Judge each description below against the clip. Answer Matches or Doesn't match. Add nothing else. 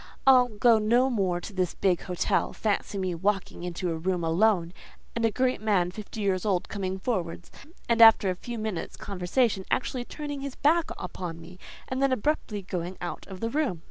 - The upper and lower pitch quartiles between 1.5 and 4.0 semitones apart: Doesn't match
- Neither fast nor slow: Matches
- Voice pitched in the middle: Doesn't match